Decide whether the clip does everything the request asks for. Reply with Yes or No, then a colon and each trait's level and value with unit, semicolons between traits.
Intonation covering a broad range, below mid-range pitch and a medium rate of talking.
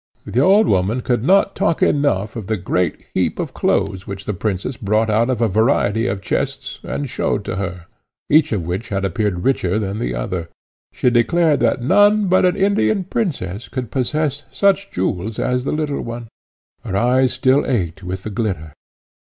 Yes: wide, 6.5 semitones; low, 115 Hz; average, 185 wpm